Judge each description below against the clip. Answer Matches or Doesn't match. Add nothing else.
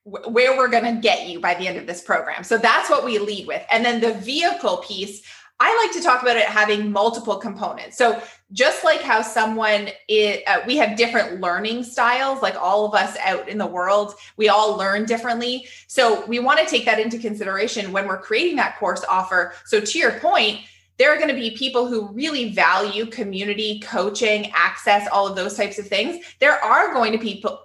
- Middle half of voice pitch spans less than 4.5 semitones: Matches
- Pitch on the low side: Doesn't match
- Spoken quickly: Matches